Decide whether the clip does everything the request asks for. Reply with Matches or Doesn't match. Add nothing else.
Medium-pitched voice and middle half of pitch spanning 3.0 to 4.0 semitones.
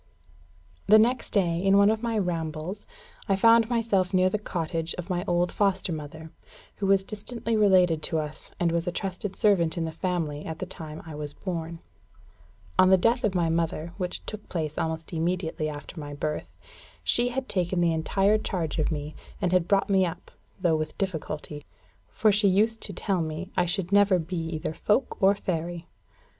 Matches